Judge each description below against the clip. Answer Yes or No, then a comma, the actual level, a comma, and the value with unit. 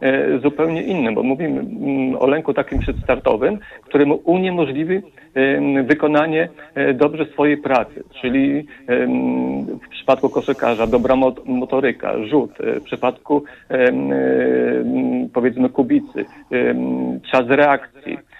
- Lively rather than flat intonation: No, average, 3.8 semitones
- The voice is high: No, low, 135 Hz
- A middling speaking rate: No, slow, 90 wpm